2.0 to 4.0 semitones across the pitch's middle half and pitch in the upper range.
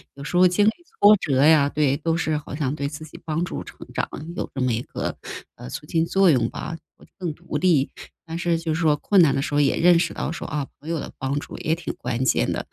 No: average, 3.1 semitones; medium, 155 Hz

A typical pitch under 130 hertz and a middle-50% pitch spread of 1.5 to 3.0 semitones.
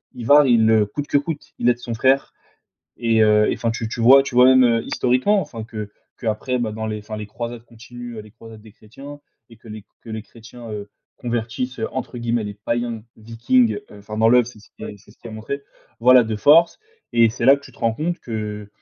Yes: low, 115 Hz; narrow, 2.4 semitones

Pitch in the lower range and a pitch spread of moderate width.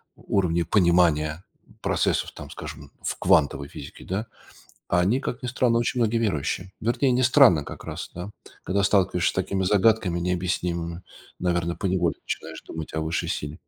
Yes: very low, 90 Hz; average, 4.1 semitones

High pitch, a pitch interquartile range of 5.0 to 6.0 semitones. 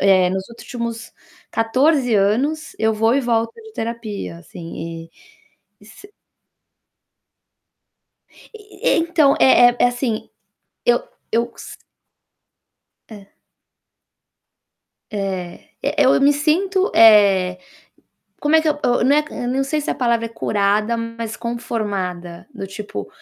Yes: high, 230 Hz; average, 5.3 semitones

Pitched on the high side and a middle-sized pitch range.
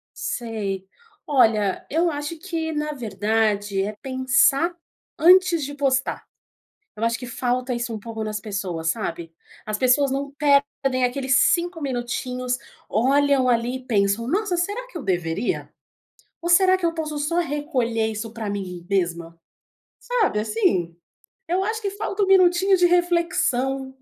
No: very high, 260 Hz; wide, 7.1 semitones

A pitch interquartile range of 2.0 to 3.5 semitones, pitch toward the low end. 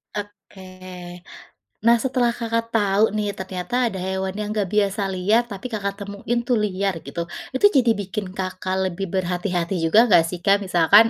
No: average, 2.7 semitones; high, 200 Hz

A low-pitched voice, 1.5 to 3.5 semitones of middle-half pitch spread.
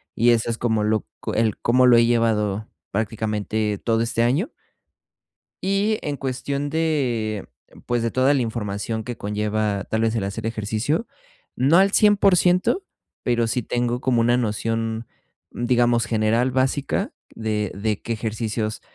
Yes: low, 115 Hz; average, 2.9 semitones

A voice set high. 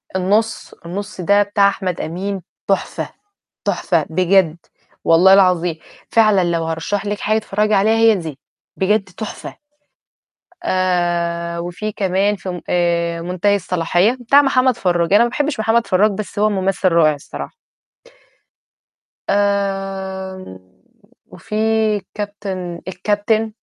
Yes: high, 195 Hz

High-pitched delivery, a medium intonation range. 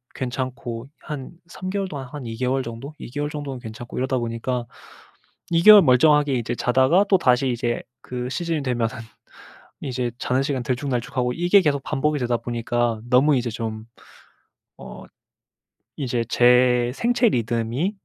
No: low, 125 Hz; average, 3.3 semitones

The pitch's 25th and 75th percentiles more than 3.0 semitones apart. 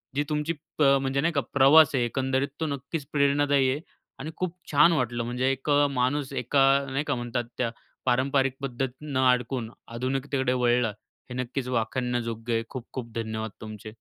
No: narrow, 2.5 semitones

